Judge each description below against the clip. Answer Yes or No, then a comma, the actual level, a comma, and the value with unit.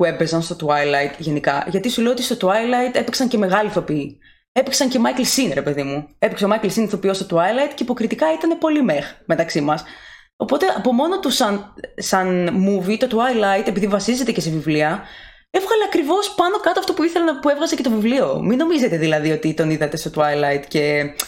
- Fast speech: Yes, fast, 195 wpm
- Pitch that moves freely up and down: Yes, wide, 8.5 semitones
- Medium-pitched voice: No, high, 205 Hz